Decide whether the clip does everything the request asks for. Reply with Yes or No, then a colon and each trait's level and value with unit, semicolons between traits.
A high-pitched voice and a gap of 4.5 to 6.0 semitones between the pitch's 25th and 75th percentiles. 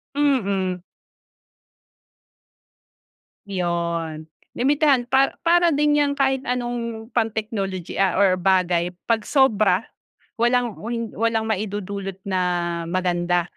Yes: high, 215 Hz; average, 5.1 semitones